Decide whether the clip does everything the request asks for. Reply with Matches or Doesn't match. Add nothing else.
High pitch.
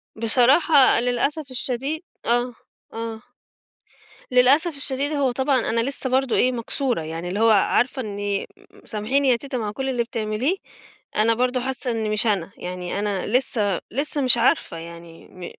Matches